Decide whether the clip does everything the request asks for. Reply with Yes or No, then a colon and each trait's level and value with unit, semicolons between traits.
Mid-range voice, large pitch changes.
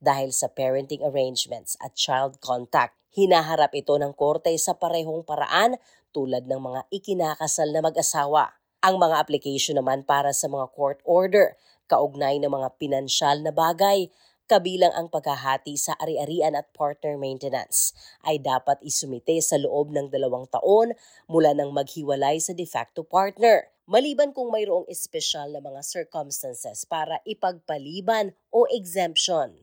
No: medium, 150 Hz; average, 4.1 semitones